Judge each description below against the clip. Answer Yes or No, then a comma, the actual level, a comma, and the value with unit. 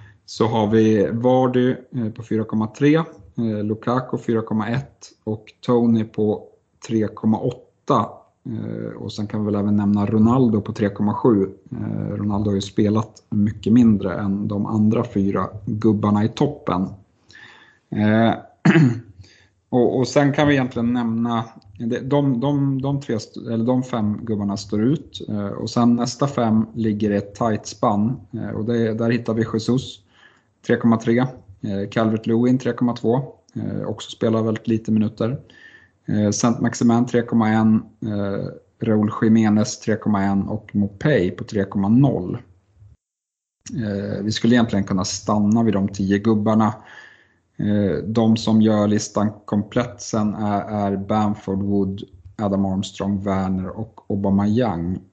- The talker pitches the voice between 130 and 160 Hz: No, low, 110 Hz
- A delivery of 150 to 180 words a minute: No, slow, 125 wpm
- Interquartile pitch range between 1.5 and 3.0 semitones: Yes, narrow, 2.5 semitones